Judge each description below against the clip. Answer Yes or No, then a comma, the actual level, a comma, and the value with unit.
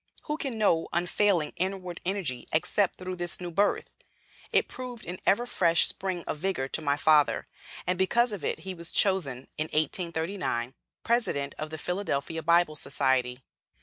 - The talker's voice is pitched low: No, medium, 175 Hz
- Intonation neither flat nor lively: Yes, average, 4.0 semitones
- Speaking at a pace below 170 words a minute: Yes, average, 160 wpm